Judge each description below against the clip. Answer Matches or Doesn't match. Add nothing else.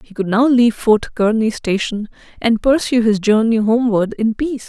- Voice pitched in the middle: Doesn't match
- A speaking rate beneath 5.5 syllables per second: Matches